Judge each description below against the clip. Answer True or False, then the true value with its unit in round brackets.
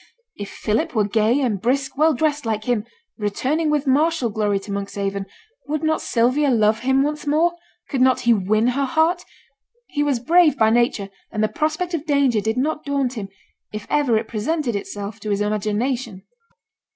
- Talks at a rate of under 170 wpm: False (180 wpm)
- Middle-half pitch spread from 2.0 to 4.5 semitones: False (5.5 semitones)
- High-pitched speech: True (245 Hz)